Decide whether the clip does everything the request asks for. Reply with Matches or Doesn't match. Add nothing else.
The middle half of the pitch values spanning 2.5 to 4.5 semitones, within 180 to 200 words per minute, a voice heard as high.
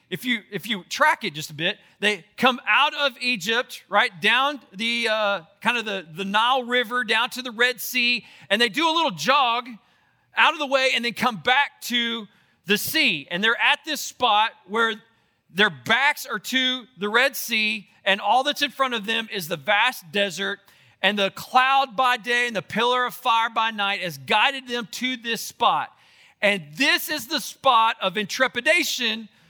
Matches